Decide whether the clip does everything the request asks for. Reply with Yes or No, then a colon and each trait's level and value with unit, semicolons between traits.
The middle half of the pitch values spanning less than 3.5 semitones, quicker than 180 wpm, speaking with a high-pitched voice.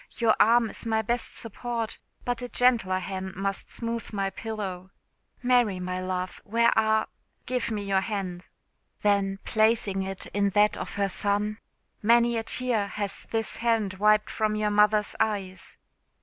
No: average, 2.7 semitones; average, 155 wpm; high, 210 Hz